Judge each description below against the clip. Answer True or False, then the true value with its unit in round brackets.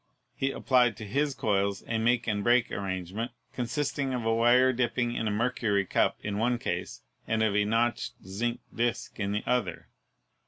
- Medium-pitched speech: False (115 Hz)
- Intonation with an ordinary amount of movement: True (3.1 semitones)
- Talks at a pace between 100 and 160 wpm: False (180 wpm)